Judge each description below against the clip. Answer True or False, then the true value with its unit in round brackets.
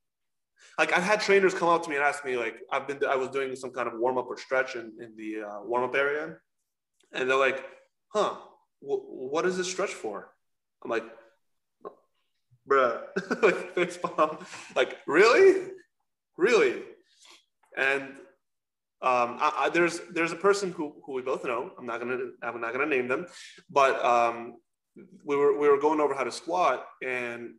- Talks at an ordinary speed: True (175 wpm)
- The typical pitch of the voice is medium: True (145 Hz)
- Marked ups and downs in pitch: True (7.4 semitones)